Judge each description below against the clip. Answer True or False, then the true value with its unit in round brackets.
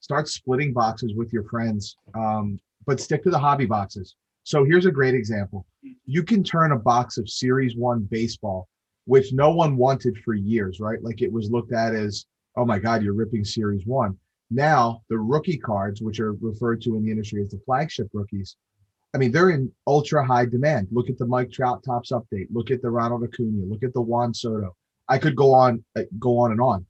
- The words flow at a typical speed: False (210 wpm)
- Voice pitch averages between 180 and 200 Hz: False (115 Hz)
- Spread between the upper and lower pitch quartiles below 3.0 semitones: False (3.3 semitones)